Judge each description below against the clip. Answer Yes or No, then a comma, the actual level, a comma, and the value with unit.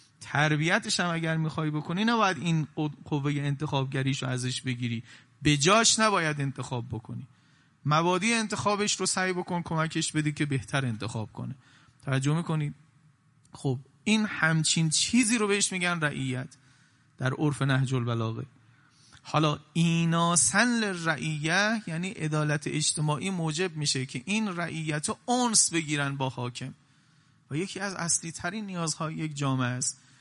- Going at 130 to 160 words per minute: Yes, average, 135 wpm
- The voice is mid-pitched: Yes, medium, 155 Hz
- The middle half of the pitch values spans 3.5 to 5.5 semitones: Yes, average, 4.3 semitones